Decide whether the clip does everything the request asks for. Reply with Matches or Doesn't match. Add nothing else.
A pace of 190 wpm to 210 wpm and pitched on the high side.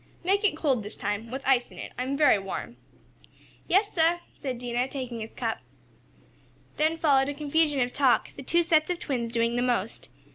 Matches